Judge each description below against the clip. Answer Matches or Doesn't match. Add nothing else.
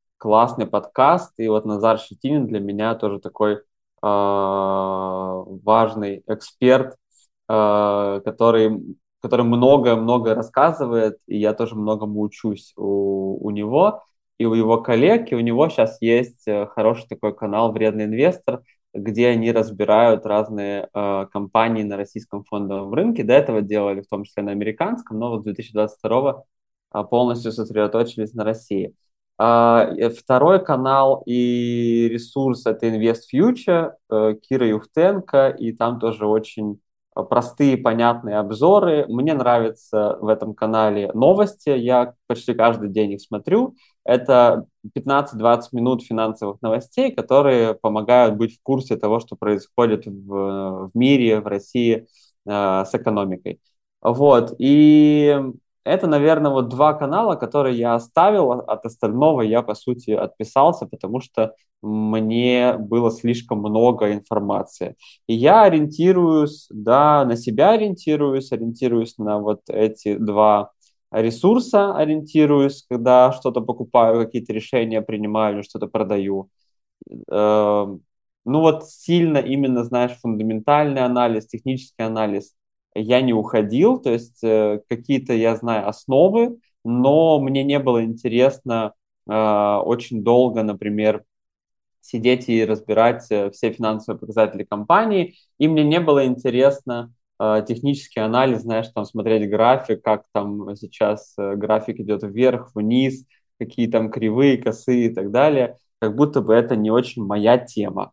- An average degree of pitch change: Matches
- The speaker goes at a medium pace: Matches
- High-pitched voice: Doesn't match